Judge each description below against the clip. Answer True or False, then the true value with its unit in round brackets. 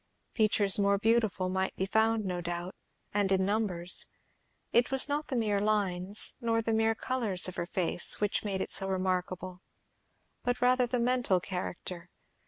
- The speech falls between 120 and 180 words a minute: True (165 wpm)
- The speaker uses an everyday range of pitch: True (3.5 semitones)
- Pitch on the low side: False (200 Hz)